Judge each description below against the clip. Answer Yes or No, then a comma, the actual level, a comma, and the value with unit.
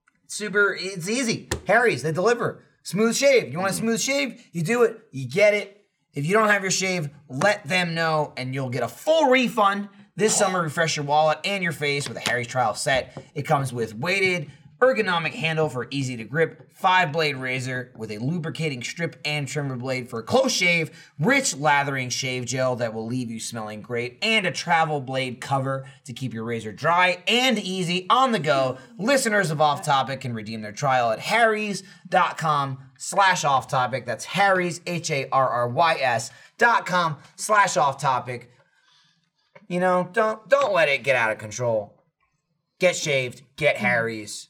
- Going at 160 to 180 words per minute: Yes, average, 175 wpm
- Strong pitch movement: Yes, wide, 6.9 semitones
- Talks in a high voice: No, medium, 155 Hz